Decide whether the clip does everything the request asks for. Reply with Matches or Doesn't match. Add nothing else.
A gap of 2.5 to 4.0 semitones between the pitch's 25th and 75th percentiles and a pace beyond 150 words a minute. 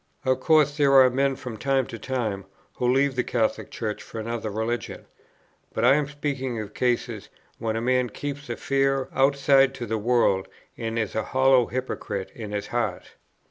Matches